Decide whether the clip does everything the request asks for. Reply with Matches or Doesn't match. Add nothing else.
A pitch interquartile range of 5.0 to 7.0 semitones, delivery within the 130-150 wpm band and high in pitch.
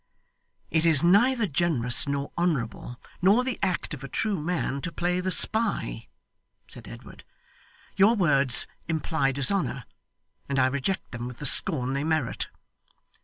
Doesn't match